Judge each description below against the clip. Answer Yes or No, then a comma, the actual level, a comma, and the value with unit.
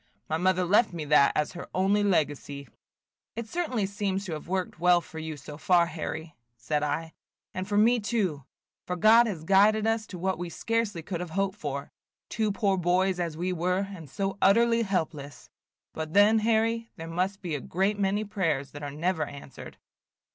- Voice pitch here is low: No, medium, 185 Hz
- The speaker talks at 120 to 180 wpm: No, average, 190 wpm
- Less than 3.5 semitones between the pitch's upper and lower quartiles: No, average, 4.3 semitones